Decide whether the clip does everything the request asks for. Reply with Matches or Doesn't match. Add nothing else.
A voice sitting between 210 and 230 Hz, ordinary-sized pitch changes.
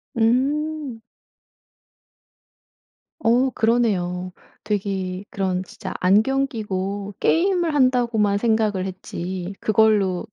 Matches